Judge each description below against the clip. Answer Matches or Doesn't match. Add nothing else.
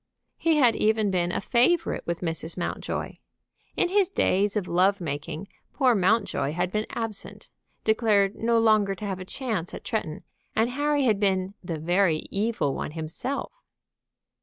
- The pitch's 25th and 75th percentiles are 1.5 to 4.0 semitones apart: Doesn't match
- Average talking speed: Matches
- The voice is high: Matches